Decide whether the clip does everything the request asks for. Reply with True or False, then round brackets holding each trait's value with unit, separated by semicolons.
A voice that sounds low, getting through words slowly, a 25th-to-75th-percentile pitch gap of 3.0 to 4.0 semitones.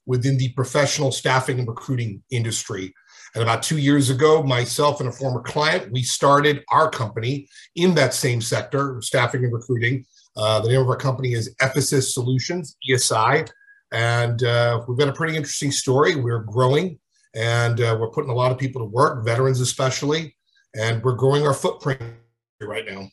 False (130 Hz; 175 wpm; 3.3 semitones)